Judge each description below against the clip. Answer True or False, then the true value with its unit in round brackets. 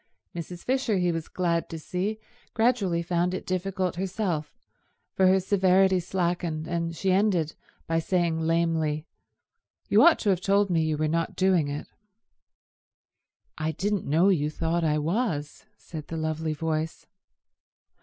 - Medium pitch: True (170 Hz)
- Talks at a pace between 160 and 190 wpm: False (145 wpm)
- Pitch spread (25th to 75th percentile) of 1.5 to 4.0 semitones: True (2.9 semitones)